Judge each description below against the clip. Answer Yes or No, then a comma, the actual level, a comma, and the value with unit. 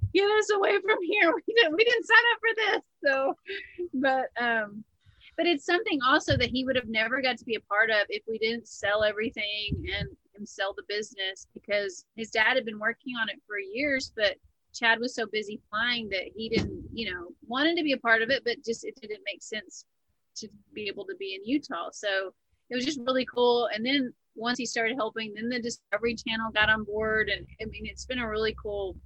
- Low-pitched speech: No, high, 230 Hz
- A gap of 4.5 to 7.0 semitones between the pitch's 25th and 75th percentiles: Yes, average, 4.8 semitones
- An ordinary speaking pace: No, fast, 225 wpm